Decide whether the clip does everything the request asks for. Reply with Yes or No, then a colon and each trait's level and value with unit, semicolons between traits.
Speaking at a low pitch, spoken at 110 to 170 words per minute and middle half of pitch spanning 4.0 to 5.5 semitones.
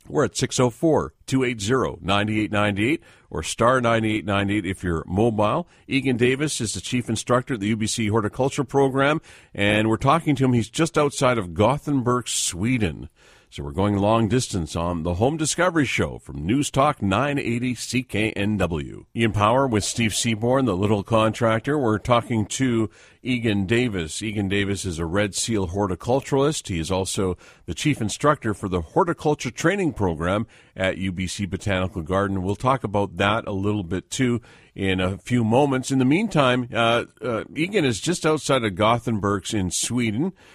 Yes: low, 110 Hz; average, 160 wpm; average, 4.5 semitones